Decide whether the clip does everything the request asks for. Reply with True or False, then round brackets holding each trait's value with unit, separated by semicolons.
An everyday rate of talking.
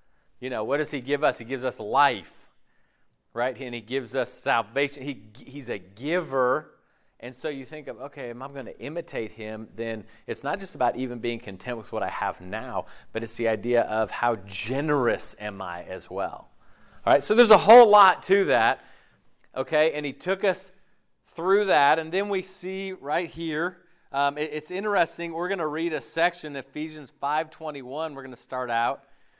True (195 wpm)